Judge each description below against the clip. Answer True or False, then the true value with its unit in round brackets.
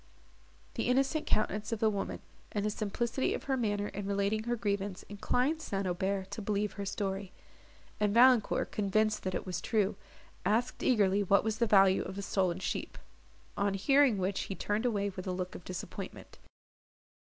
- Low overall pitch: False (205 Hz)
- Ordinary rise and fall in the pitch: False (2.2 semitones)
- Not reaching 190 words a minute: True (175 wpm)